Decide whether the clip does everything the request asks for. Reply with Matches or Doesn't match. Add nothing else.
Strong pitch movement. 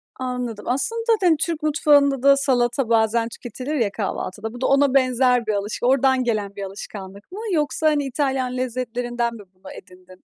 Doesn't match